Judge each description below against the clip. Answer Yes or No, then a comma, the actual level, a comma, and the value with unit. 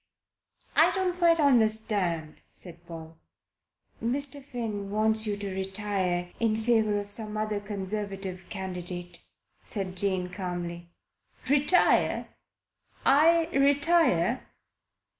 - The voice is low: No, high, 205 Hz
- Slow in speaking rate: Yes, slow, 100 wpm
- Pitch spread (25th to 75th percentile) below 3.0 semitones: No, average, 4.9 semitones